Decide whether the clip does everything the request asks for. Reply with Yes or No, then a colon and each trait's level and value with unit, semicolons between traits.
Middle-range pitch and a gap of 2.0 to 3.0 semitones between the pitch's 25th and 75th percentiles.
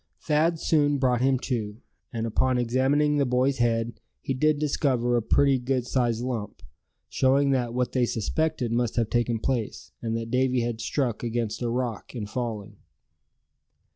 No: low, 125 Hz; narrow, 2.5 semitones